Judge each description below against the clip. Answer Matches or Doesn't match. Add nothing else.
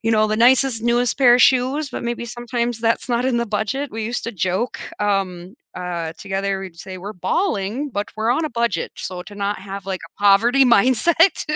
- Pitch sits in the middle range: Doesn't match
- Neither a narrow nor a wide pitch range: Matches